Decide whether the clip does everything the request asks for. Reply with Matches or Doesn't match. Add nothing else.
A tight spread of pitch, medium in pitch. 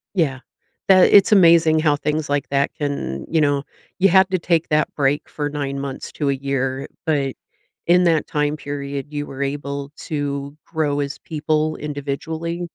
Matches